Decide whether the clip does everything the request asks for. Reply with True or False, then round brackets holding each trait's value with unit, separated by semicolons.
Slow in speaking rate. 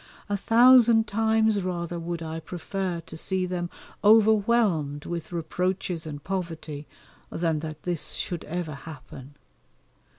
True (125 wpm)